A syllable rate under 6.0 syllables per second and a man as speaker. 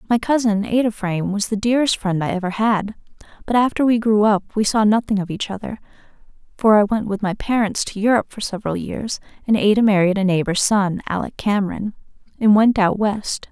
No: 5.8 syllables/s; female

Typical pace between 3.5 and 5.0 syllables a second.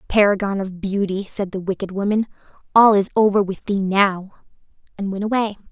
No: 5.4 syllables/s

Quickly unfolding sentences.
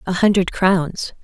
No: average, 145 wpm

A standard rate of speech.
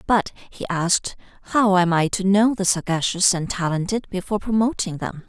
Yes: average, 170 wpm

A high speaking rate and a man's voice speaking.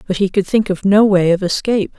No: fast, 270 wpm; female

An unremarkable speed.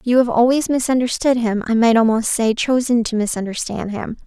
Yes: average, 185 wpm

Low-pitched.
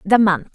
No: high, 200 Hz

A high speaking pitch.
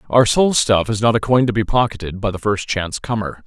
No: low, 110 Hz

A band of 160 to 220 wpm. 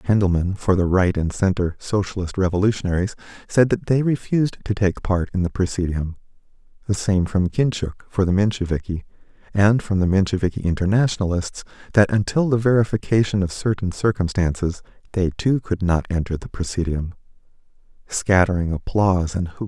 No: average, 145 wpm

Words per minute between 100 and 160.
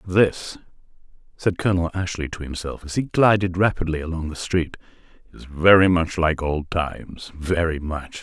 Yes: average, 145 wpm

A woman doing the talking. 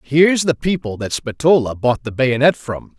No: male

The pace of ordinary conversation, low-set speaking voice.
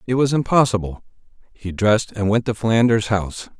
Yes: average, 165 wpm; low, 110 Hz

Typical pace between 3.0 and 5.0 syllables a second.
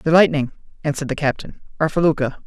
No: 6.8 syllables/s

